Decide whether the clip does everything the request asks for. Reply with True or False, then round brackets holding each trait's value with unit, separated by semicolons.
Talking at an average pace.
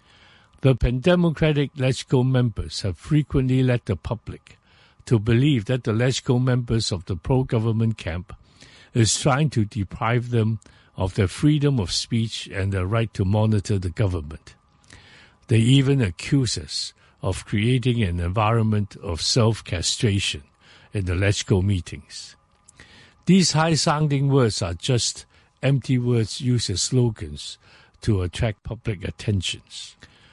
False (125 wpm)